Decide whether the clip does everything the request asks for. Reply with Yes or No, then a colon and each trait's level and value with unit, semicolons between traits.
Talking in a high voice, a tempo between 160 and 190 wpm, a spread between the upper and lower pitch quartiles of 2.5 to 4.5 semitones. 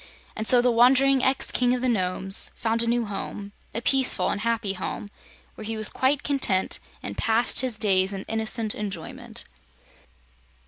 Yes: high, 225 Hz; average, 170 wpm; average, 3.6 semitones